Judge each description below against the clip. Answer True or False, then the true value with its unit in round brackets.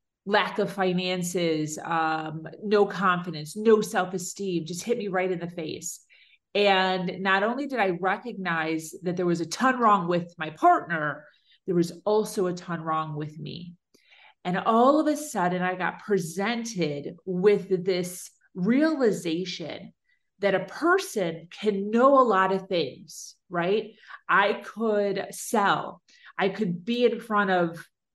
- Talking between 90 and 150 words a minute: True (145 wpm)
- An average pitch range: True (3.4 semitones)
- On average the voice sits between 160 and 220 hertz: True (190 Hz)